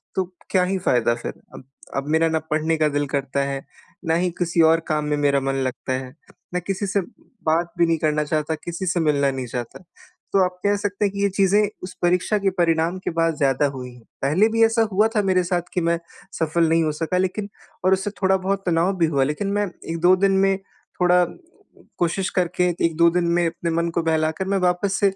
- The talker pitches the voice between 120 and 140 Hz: No, medium, 170 Hz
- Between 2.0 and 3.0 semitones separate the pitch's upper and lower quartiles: No, average, 3.7 semitones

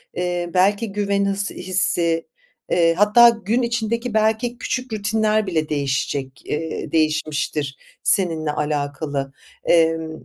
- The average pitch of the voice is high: No, medium, 180 Hz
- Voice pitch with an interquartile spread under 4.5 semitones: No, wide, 5.6 semitones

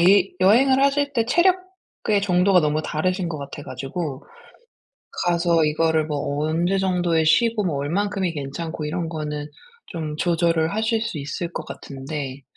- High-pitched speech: No, medium, 170 Hz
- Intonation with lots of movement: No, average, 4.7 semitones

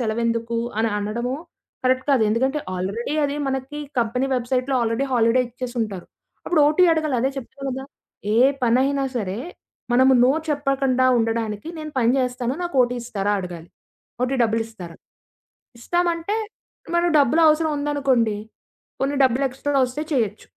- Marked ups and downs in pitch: No, average, 3.3 semitones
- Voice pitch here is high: Yes, very high, 255 Hz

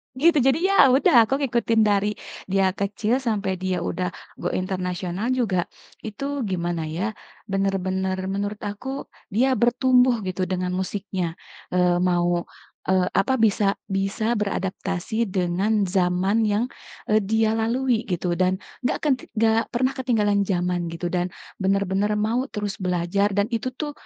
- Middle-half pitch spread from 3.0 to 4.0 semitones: Yes, average, 3.6 semitones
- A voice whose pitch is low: No, high, 200 Hz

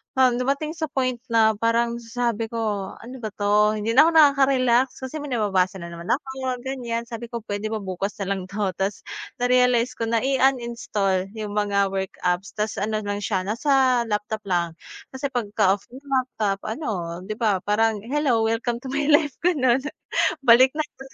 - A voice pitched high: Yes, high, 230 Hz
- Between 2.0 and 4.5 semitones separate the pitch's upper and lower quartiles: Yes, average, 3.9 semitones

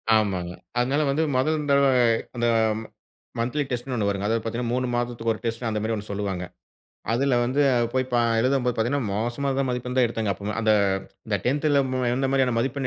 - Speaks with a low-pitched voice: Yes, low, 120 Hz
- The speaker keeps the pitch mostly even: No, average, 3.3 semitones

